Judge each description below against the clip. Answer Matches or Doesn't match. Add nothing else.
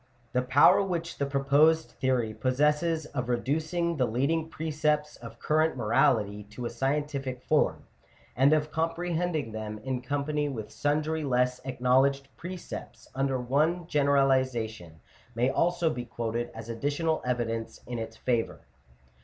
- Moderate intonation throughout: Matches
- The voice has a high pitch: Doesn't match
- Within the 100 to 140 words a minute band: Matches